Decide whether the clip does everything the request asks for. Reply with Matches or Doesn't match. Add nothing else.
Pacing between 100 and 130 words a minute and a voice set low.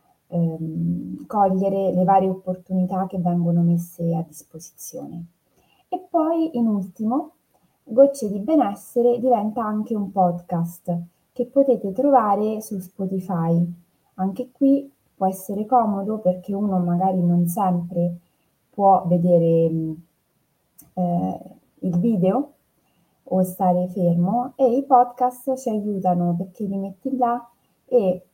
Doesn't match